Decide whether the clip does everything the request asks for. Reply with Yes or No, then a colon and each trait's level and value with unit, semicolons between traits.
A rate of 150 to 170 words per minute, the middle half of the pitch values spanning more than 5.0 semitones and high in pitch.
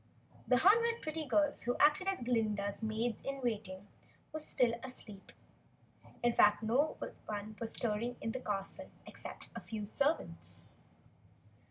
No: average, 140 wpm; wide, 5.5 semitones; high, 240 Hz